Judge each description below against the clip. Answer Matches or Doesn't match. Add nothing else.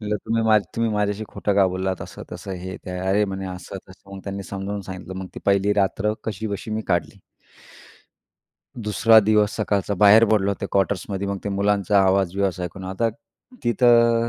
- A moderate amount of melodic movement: Doesn't match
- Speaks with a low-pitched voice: Matches